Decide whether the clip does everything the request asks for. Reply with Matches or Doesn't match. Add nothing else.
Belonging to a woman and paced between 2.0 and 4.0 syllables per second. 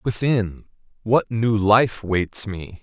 Doesn't match